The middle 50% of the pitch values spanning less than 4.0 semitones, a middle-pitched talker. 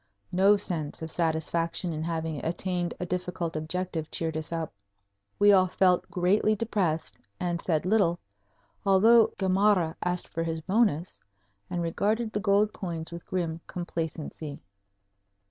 Yes: average, 3.0 semitones; medium, 175 Hz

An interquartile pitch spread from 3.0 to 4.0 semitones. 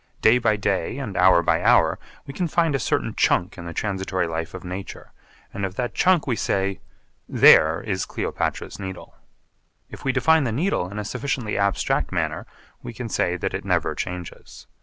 No: wide, 5.4 semitones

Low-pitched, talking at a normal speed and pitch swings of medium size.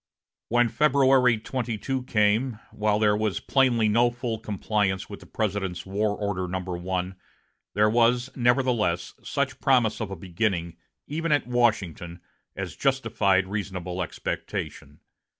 No: low, 105 Hz; slow, 130 wpm; average, 4.3 semitones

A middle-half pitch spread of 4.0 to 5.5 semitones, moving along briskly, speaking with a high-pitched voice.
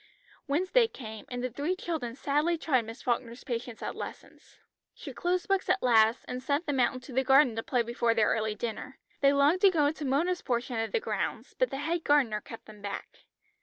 Yes: average, 5.2 semitones; fast, 210 wpm; very high, 265 Hz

